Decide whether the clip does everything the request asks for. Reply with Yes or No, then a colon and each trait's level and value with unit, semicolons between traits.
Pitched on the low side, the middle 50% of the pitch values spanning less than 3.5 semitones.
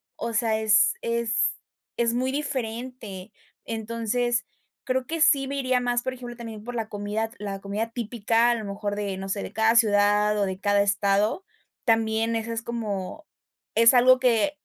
No: high, 225 Hz; average, 2.8 semitones